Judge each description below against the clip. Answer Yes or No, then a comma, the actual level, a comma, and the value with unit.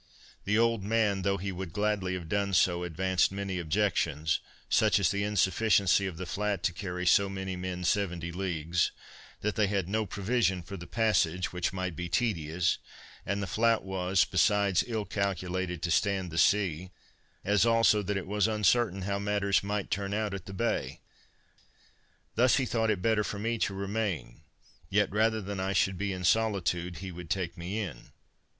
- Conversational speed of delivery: Yes, average, 180 wpm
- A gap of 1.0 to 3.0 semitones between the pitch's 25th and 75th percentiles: Yes, narrow, 2.6 semitones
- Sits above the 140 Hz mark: No, very low, 95 Hz